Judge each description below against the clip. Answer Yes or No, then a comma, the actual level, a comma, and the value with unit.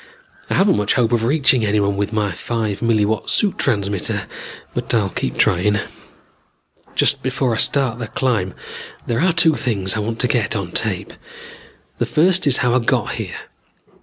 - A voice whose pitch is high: No, low, 115 Hz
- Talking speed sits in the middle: Yes, average, 170 wpm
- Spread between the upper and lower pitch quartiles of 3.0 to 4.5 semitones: Yes, average, 4.0 semitones